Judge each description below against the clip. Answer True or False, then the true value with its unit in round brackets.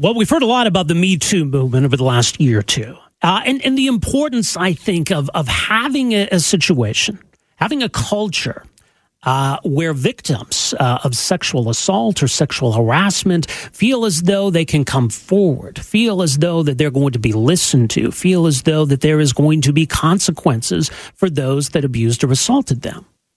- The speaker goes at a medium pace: True (195 wpm)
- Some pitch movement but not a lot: False (6.2 semitones)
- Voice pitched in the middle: True (160 Hz)